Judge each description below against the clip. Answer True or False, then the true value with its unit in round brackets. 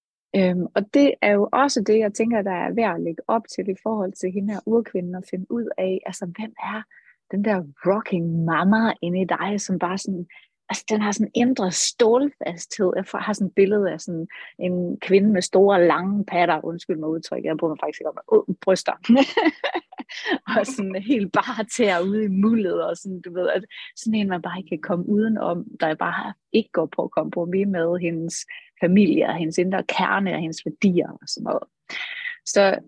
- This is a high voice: True (195 Hz)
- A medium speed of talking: True (210 wpm)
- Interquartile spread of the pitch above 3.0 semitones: True (3.4 semitones)